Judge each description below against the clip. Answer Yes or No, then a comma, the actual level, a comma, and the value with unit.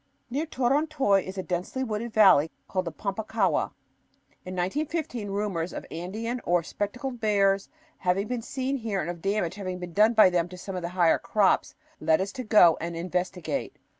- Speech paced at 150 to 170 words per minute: No, average, 185 wpm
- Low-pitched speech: No, high, 195 Hz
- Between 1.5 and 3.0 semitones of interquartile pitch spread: No, average, 4.2 semitones